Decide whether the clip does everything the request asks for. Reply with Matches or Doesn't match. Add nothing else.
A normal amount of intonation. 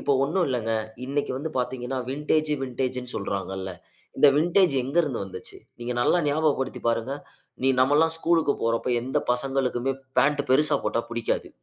Matches